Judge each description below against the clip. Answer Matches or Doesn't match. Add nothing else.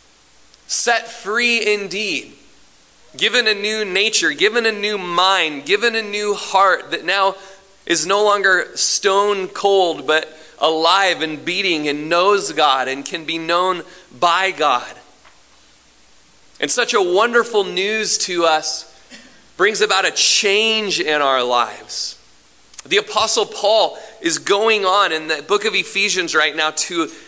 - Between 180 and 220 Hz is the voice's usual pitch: Matches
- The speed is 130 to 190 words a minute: Matches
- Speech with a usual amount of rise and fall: Matches